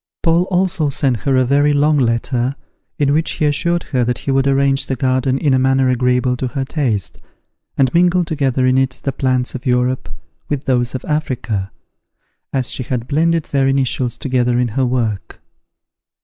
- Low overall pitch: Yes, low, 130 Hz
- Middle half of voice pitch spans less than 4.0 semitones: Yes, narrow, 2.4 semitones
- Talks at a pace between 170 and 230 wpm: Yes, average, 180 wpm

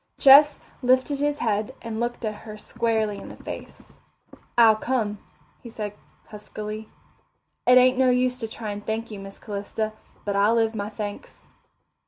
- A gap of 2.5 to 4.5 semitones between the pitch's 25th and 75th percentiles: Yes, average, 3.0 semitones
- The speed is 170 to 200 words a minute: No, average, 160 wpm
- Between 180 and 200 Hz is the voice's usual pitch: No, high, 220 Hz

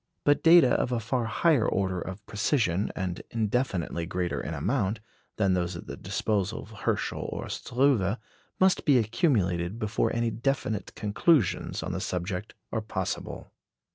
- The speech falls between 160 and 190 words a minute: No, average, 150 wpm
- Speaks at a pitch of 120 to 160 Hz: No, low, 105 Hz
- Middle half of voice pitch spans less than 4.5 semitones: No, average, 4.8 semitones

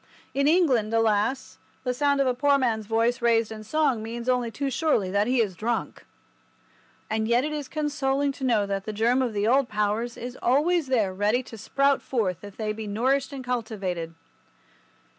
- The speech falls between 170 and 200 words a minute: Yes, average, 190 wpm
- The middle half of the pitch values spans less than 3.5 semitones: No, average, 3.9 semitones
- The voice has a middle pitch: No, high, 235 Hz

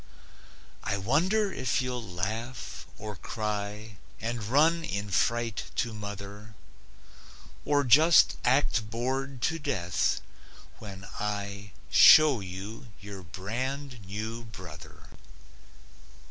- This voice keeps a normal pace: No, slow, 100 wpm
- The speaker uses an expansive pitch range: No, average, 4.3 semitones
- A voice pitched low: Yes, low, 110 Hz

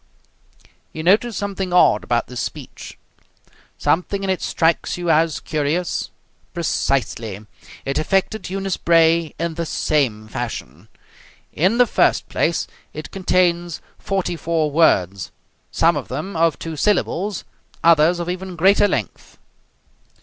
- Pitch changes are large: No, average, 3.6 semitones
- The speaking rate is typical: No, slow, 130 wpm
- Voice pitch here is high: No, medium, 170 Hz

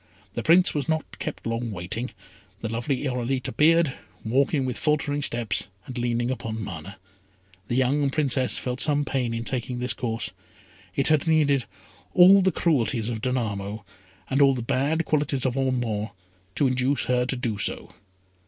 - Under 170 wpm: Yes, average, 160 wpm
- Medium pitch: No, low, 130 Hz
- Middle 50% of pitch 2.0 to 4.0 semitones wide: Yes, average, 3.5 semitones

